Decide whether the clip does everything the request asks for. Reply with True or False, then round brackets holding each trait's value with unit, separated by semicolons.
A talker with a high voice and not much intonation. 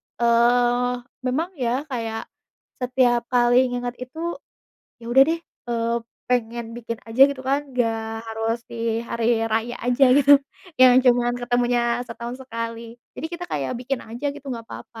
True (240 Hz; 1.4 semitones)